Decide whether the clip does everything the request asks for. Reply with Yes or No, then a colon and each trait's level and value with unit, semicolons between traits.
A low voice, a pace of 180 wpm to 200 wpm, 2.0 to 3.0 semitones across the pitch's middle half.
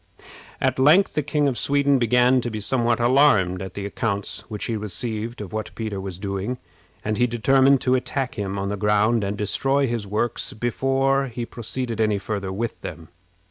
No: low, 115 Hz; average, 185 wpm; average, 4.2 semitones